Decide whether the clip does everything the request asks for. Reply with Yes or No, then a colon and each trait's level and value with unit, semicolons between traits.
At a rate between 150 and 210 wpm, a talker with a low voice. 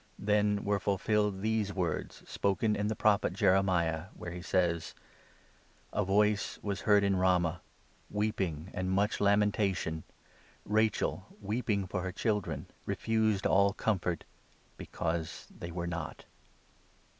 No: slow, 135 wpm; low, 100 Hz